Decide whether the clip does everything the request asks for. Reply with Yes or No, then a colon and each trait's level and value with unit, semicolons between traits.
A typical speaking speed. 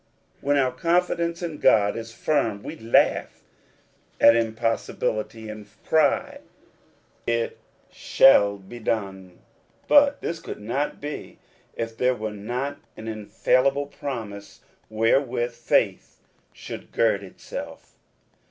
No: slow, 115 wpm